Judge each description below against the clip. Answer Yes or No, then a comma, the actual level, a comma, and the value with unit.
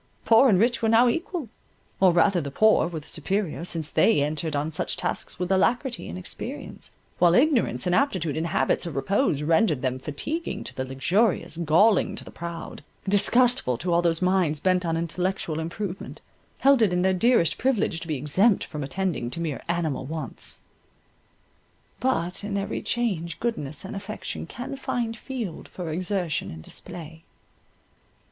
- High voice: No, medium, 180 Hz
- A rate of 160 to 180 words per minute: Yes, average, 165 wpm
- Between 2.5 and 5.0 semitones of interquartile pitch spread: No, wide, 5.6 semitones